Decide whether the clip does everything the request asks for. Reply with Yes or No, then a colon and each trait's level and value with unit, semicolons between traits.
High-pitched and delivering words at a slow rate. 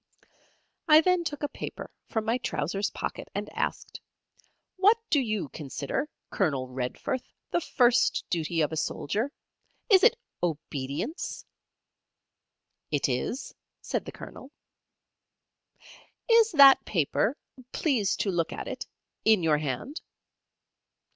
Yes: high, 215 Hz; slow, 120 wpm